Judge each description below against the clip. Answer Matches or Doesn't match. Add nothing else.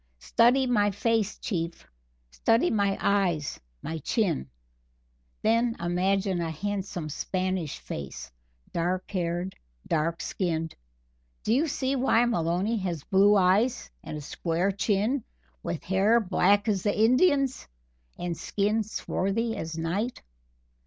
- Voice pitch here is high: Matches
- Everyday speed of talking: Doesn't match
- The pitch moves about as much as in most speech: Matches